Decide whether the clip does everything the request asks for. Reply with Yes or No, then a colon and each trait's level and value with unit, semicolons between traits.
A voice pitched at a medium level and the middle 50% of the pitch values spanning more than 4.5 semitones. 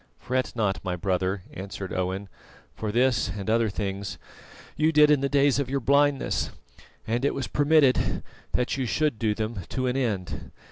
No: low, 120 Hz; wide, 5.6 semitones